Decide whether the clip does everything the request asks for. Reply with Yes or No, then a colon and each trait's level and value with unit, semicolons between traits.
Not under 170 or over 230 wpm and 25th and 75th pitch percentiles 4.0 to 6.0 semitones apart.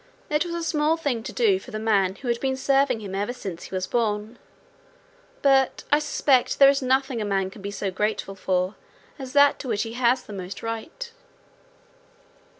Yes: average, 200 wpm; average, 5.2 semitones